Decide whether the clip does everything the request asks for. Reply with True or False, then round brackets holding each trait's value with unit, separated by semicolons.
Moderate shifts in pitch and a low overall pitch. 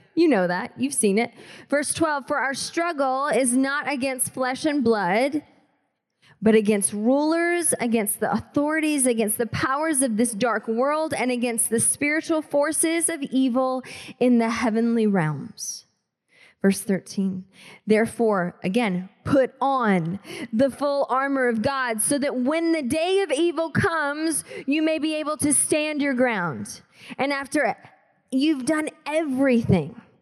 False (4.7 semitones; 265 Hz)